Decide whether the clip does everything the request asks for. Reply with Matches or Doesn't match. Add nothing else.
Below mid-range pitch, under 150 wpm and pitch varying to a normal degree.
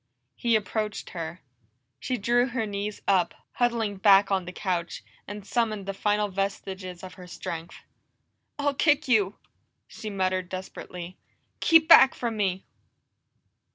Doesn't match